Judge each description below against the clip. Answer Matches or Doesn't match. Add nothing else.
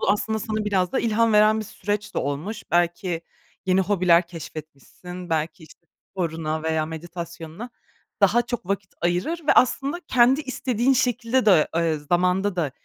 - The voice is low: Doesn't match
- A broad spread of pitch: Doesn't match